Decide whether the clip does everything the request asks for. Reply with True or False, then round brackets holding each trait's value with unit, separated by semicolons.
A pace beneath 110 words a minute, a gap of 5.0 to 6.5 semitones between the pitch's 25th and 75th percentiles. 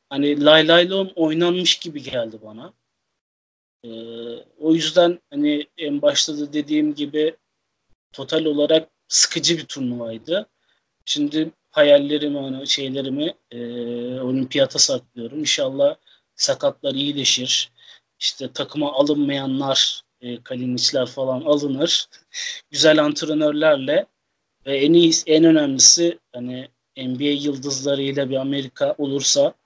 False (100 wpm; 3.6 semitones)